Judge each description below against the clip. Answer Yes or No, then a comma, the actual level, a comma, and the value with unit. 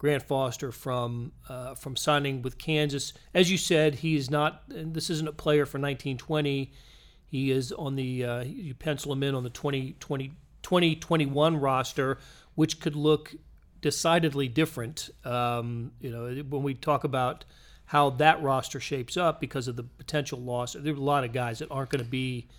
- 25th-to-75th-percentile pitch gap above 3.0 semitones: No, narrow, 2.6 semitones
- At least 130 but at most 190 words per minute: Yes, average, 185 wpm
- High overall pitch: No, medium, 140 Hz